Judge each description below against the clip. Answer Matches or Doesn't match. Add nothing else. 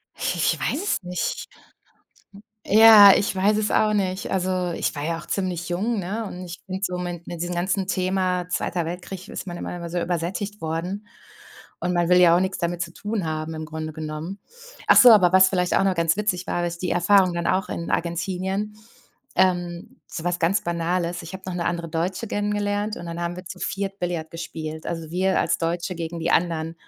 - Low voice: Doesn't match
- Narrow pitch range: Matches